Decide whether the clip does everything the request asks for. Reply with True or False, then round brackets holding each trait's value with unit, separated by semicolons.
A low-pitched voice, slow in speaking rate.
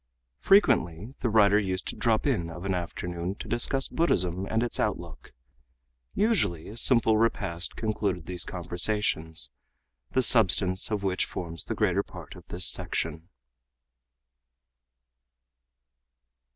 True (95 Hz; 125 wpm)